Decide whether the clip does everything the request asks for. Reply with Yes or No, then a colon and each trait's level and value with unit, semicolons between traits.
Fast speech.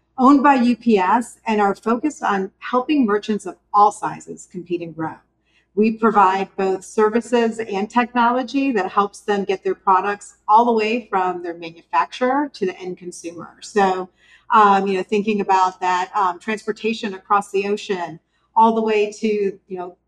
No: average, 165 wpm